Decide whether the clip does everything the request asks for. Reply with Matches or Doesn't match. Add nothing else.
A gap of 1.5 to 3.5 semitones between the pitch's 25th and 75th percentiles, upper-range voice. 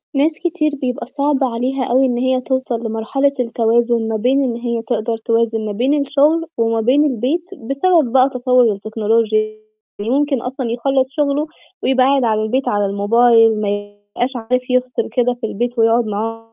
Matches